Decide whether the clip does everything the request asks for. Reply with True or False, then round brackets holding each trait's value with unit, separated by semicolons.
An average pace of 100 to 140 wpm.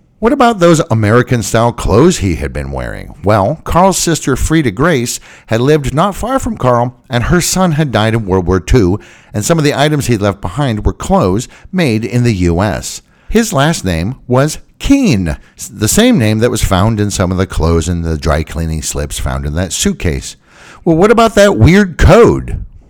False (195 wpm)